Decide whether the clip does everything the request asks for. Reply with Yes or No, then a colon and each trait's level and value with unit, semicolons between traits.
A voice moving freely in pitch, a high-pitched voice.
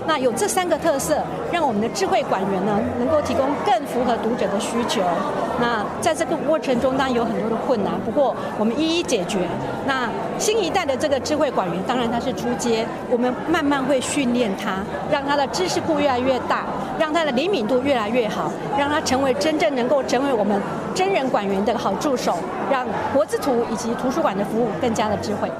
No: average, 4.6 semitones; very high, 265 Hz